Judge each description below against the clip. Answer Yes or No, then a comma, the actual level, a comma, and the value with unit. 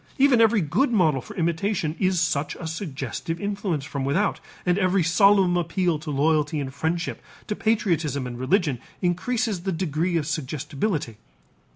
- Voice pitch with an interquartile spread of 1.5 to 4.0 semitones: No, average, 4.8 semitones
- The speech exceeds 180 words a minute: No, average, 155 wpm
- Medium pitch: Yes, medium, 170 Hz